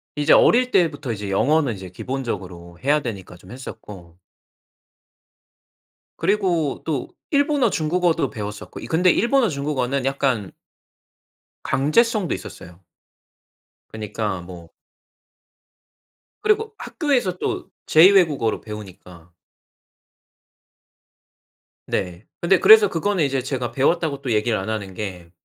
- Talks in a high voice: No, low, 135 Hz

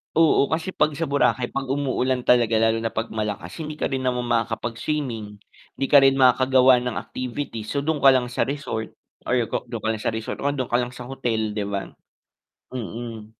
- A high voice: No, low, 125 Hz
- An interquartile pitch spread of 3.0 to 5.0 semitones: Yes, average, 3.3 semitones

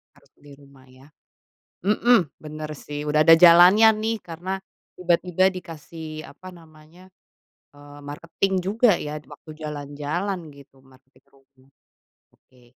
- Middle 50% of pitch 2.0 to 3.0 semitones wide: No, average, 3.9 semitones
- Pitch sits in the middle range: Yes, medium, 155 Hz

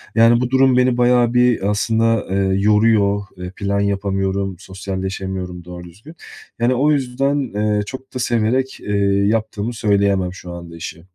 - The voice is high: No, low, 105 Hz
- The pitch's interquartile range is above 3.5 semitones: Yes, average, 4.1 semitones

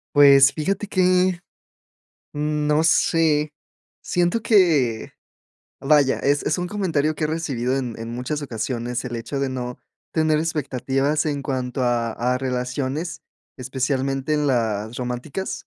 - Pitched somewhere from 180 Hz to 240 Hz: No, medium, 140 Hz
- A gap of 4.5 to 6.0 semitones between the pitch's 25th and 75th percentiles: No, average, 3.7 semitones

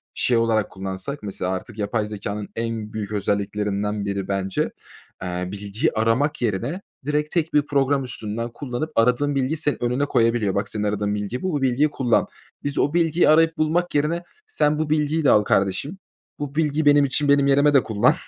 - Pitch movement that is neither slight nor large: No, wide, 6.0 semitones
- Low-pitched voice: Yes, low, 120 Hz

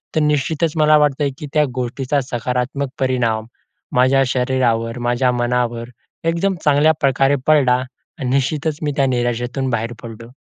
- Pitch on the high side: No, low, 130 Hz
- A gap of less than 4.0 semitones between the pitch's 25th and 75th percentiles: Yes, average, 3.1 semitones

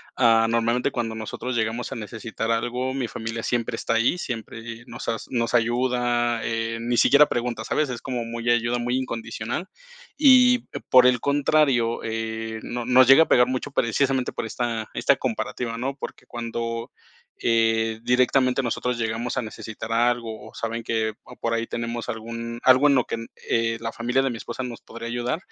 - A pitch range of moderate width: No, narrow, 1.6 semitones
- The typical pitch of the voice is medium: No, low, 120 Hz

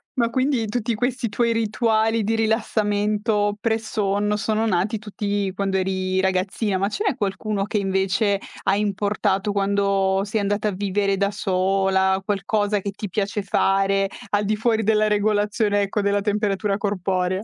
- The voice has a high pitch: Yes, high, 205 Hz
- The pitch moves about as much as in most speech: No, narrow, 1.7 semitones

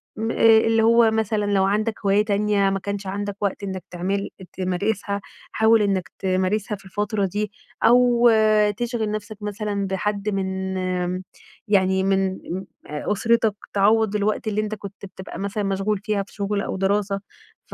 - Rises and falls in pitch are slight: Yes, narrow, 1.7 semitones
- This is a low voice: No, high, 205 Hz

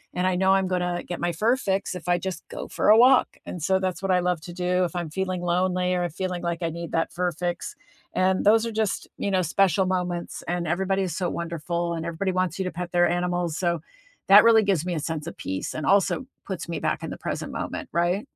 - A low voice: No, medium, 180 Hz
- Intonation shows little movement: Yes, narrow, 1.8 semitones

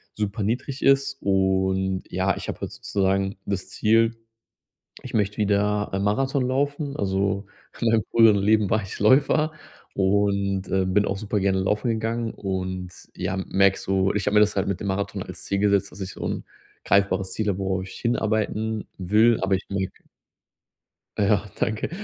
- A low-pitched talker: Yes, low, 100 Hz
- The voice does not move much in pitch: Yes, narrow, 2.3 semitones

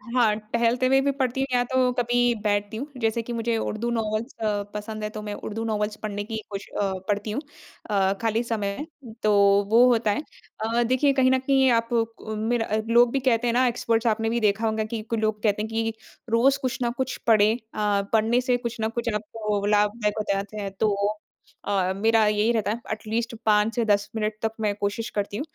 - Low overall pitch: No, high, 225 Hz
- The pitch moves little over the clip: Yes, narrow, 2.1 semitones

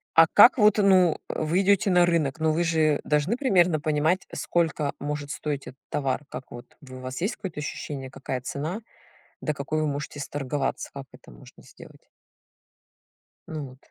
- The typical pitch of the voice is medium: Yes, medium, 150 Hz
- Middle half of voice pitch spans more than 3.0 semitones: Yes, average, 3.7 semitones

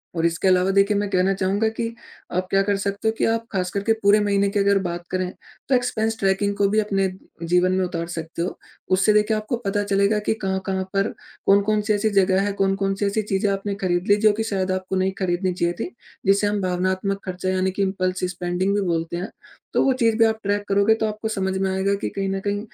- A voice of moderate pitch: No, high, 195 Hz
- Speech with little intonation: Yes, narrow, 1.6 semitones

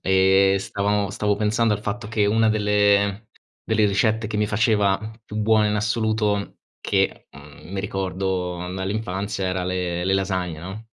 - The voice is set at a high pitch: No, low, 100 Hz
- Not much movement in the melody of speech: Yes, narrow, 2.0 semitones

